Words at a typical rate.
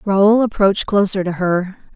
Yes: average, 155 wpm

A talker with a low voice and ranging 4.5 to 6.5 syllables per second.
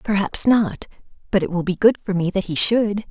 No: high, 195 Hz; 5.4 syllables/s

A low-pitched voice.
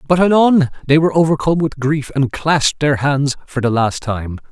No: medium, 145 Hz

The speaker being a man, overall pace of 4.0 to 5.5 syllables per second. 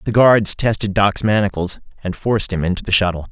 No: male; 5.8 syllables/s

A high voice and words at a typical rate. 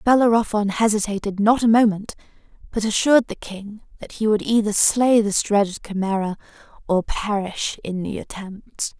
Yes: high, 210 Hz; average, 145 wpm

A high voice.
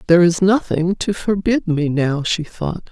No: medium, 175 Hz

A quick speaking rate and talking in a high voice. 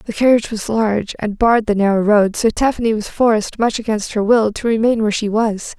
Yes: fast, 230 wpm; high, 220 Hz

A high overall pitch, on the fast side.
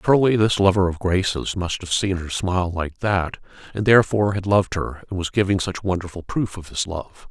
No: very low, 95 Hz; fast, 215 wpm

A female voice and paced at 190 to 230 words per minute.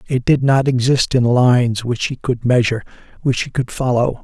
No: male; average, 200 wpm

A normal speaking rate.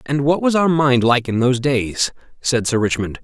No: fast, 220 wpm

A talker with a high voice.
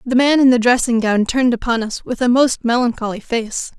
Yes: high, 240 Hz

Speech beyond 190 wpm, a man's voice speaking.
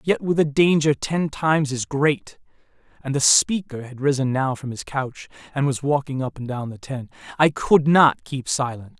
Yes: average, 200 wpm; male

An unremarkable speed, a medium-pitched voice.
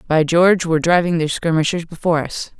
Yes: average, 185 wpm; medium, 165 Hz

